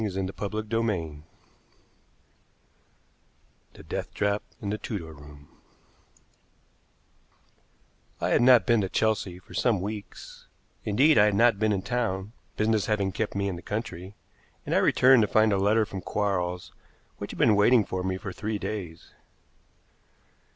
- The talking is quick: No, average, 145 wpm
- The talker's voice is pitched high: No, low, 105 Hz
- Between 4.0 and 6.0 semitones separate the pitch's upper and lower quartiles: No, narrow, 2.6 semitones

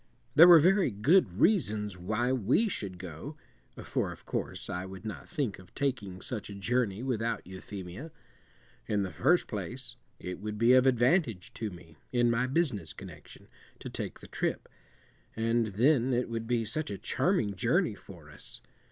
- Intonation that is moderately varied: Yes, average, 4.9 semitones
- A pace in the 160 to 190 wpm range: Yes, average, 170 wpm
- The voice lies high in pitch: No, low, 115 Hz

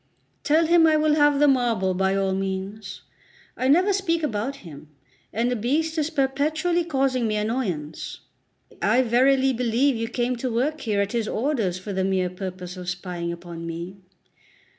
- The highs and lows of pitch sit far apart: Yes, wide, 6.9 semitones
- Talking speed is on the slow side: No, average, 170 wpm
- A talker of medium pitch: No, high, 235 Hz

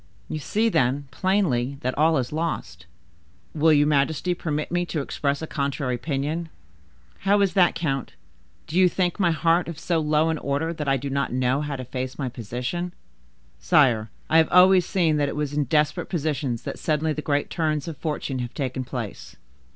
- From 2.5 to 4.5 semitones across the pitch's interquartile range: Yes, average, 3.5 semitones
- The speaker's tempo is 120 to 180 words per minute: No, average, 190 wpm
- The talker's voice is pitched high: No, medium, 150 Hz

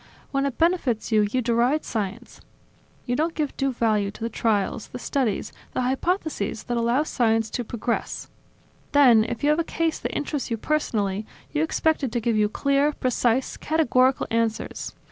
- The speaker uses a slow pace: No, average, 175 wpm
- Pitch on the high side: Yes, high, 245 Hz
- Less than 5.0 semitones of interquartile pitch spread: Yes, average, 4.5 semitones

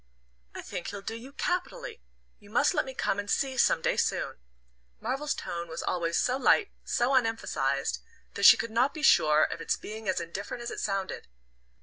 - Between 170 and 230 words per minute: Yes, average, 195 wpm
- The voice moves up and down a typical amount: No, wide, 5.9 semitones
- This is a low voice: No, high, 225 Hz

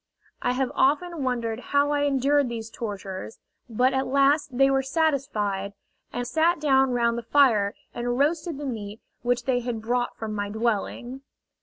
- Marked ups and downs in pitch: No, average, 3.6 semitones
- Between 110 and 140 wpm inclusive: No, average, 165 wpm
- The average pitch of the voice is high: Yes, very high, 250 Hz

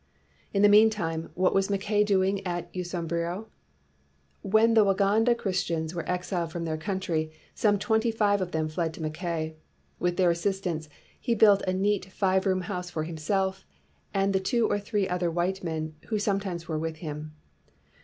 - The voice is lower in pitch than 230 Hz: Yes, medium, 185 Hz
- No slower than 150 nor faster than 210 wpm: Yes, average, 175 wpm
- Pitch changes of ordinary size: Yes, average, 3.3 semitones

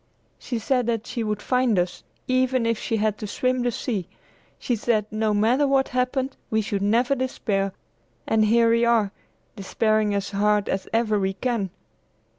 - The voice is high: Yes, high, 225 Hz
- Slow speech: No, average, 175 wpm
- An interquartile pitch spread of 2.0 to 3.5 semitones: Yes, average, 3.1 semitones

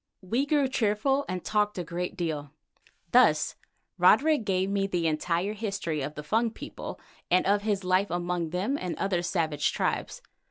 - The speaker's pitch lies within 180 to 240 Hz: Yes, medium, 185 Hz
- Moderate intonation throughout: Yes, average, 3.5 semitones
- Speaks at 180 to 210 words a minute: No, average, 165 wpm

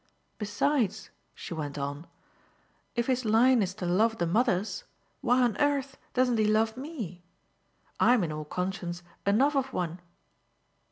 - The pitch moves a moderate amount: No, wide, 6.2 semitones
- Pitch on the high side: Yes, high, 215 Hz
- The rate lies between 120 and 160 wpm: Yes, average, 145 wpm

